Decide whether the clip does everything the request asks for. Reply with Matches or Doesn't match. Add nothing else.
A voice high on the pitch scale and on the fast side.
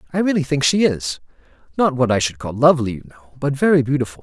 Doesn't match